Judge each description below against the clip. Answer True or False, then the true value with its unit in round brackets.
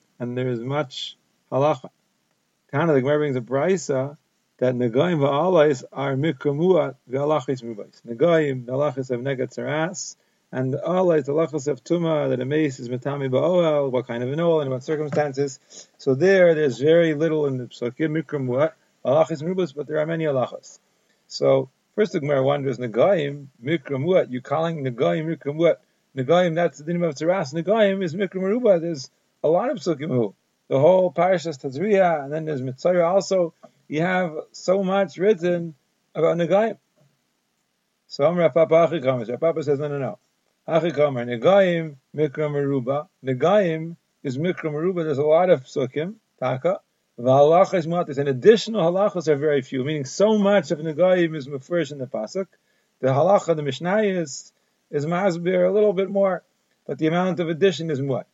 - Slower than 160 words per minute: False (165 wpm)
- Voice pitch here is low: False (155 Hz)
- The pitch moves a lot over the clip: False (4.2 semitones)